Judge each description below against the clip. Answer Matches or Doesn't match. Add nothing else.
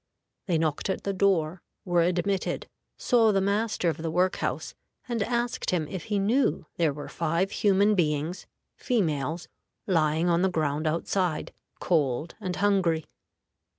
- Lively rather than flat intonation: Doesn't match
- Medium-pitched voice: Matches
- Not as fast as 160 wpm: Matches